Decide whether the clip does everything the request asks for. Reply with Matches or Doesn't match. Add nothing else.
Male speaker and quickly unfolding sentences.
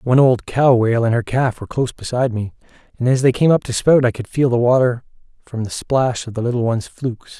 Matches